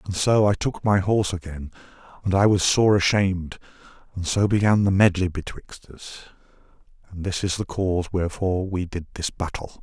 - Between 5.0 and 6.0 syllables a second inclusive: Yes, 5.5 syllables/s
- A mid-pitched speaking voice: No, very low, 95 Hz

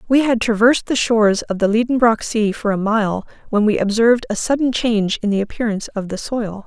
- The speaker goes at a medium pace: No, fast, 215 wpm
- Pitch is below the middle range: No, high, 220 Hz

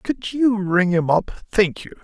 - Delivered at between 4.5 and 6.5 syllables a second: No, 3.9 syllables/s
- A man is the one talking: Yes, male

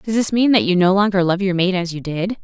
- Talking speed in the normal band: No, fast, 320 wpm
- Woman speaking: Yes, female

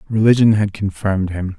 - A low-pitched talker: Yes, low, 100 Hz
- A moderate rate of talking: Yes, average, 150 wpm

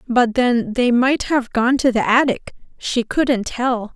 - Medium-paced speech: Yes, average, 165 wpm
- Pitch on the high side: Yes, high, 245 Hz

